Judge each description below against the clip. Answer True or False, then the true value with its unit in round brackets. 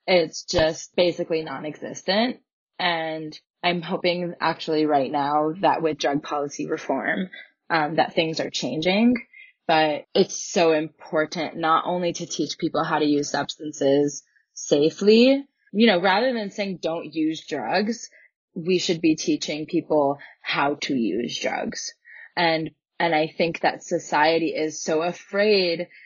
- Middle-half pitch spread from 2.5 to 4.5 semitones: True (2.9 semitones)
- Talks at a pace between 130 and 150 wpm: True (140 wpm)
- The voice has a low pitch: False (165 Hz)